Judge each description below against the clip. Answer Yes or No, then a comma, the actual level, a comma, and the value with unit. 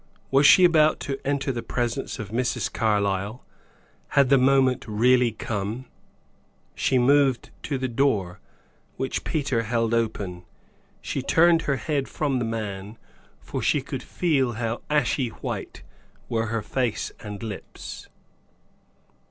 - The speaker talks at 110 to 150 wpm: Yes, slow, 135 wpm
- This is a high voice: No, low, 125 Hz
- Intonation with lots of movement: No, average, 3.7 semitones